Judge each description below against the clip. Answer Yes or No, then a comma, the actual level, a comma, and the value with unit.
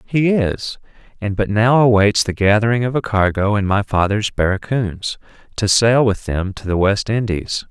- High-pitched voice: No, low, 105 Hz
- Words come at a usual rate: Yes, average, 180 wpm